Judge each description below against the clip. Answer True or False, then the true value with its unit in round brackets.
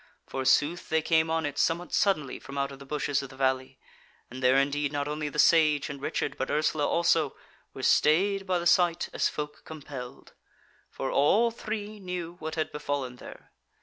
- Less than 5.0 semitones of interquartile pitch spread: True (3.3 semitones)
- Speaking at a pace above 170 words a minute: True (185 wpm)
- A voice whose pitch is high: False (150 Hz)